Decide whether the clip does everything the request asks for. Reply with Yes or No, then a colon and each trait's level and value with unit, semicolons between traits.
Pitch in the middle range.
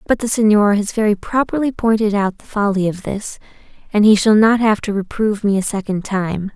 No: high, 210 Hz